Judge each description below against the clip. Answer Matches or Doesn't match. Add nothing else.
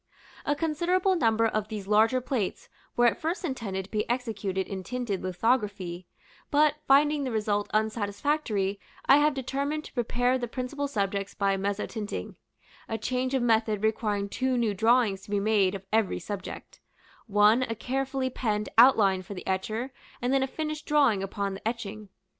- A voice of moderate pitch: Doesn't match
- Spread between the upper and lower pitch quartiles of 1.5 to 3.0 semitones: Doesn't match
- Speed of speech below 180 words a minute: Matches